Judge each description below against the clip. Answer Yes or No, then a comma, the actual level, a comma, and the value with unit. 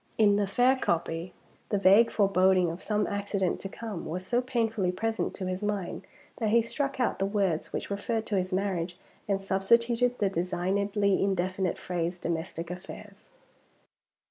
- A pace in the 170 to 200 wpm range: No, average, 160 wpm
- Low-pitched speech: No, high, 195 Hz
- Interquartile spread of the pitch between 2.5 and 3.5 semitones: Yes, average, 3.0 semitones